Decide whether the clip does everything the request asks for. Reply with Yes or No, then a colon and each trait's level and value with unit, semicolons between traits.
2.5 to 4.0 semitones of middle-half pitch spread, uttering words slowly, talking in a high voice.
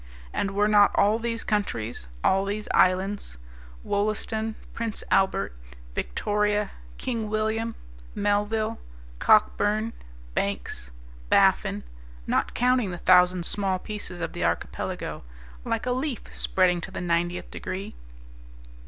Yes: average, 3.0 semitones; slow, 115 wpm; high, 205 Hz